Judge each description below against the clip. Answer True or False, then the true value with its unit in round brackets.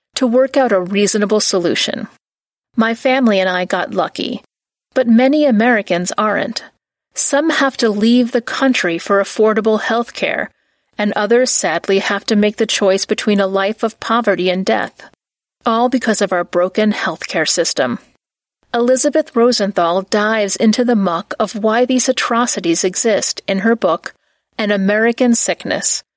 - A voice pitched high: True (220 Hz)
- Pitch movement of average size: True (3.6 semitones)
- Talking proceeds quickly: False (150 wpm)